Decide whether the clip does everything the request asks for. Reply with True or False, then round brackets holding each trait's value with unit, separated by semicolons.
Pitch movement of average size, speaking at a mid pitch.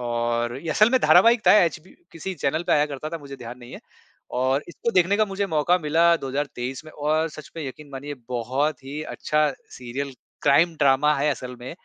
True (3.8 semitones; 150 Hz)